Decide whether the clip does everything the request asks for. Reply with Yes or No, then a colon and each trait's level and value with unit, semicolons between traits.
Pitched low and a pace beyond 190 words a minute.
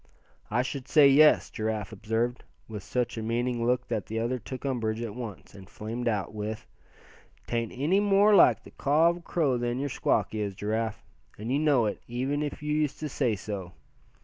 Yes: low, 120 Hz; average, 200 wpm